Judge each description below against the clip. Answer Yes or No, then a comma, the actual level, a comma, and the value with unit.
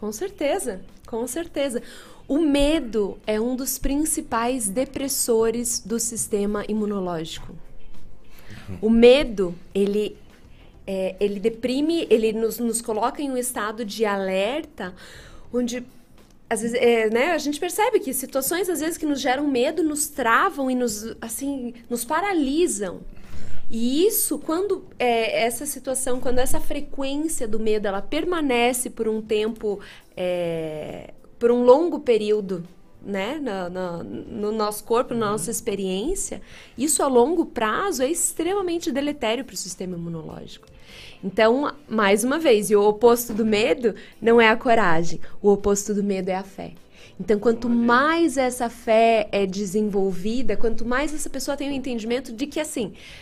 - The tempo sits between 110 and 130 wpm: No, average, 145 wpm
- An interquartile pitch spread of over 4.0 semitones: Yes, average, 5.1 semitones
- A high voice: Yes, high, 235 Hz